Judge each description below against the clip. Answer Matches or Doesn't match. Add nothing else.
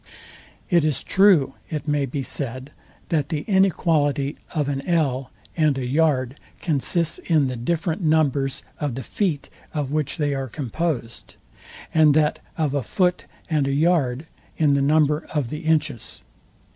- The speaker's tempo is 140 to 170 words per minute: Matches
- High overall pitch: Doesn't match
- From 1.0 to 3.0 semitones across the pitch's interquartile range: Matches